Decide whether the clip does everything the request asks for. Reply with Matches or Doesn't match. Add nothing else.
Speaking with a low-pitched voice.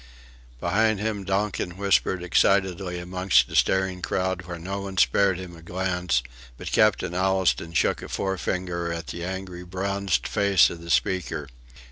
Matches